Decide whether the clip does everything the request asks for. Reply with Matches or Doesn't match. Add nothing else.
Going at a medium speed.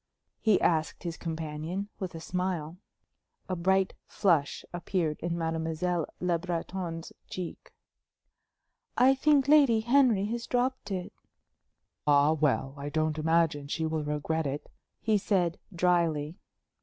Doesn't match